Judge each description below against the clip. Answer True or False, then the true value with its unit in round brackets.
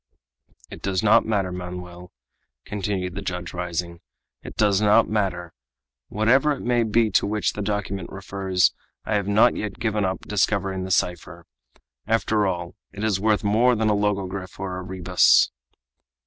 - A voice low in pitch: True (100 Hz)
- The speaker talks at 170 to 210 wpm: False (160 wpm)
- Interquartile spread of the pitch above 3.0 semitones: False (2.7 semitones)